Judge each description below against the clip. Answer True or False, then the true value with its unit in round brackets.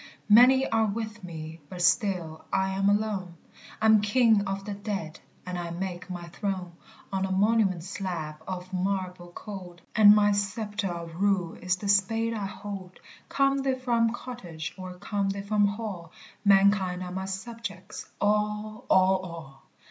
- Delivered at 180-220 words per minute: False (155 wpm)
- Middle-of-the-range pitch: False (195 Hz)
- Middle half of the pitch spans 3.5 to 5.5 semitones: False (2.7 semitones)